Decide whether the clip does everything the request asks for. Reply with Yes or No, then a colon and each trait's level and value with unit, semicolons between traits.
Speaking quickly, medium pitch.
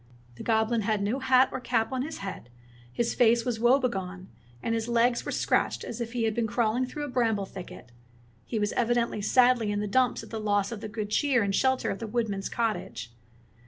No: fast, 220 wpm; high, 230 Hz